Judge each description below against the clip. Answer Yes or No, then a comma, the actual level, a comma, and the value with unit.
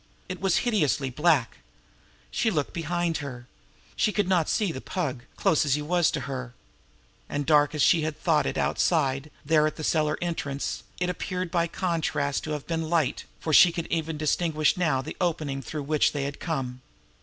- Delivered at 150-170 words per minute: No, average, 190 wpm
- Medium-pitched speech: Yes, medium, 155 Hz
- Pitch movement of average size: Yes, average, 3.2 semitones